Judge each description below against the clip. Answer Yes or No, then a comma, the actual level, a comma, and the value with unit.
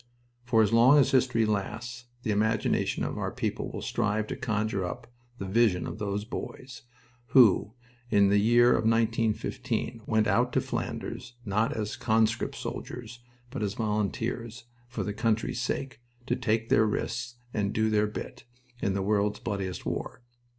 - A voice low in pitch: Yes, low, 110 Hz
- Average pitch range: No, narrow, 2.1 semitones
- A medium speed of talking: Yes, average, 165 wpm